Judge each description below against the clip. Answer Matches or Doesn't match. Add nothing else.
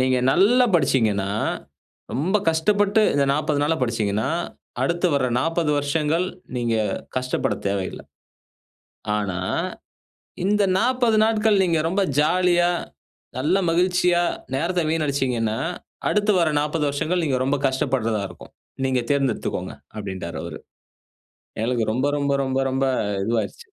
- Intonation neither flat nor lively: Doesn't match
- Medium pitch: Matches